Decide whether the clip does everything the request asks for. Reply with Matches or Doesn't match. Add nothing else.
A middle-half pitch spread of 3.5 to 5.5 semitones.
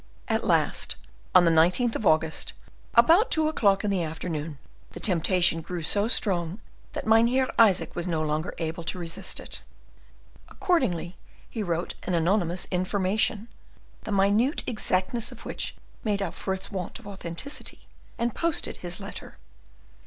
Matches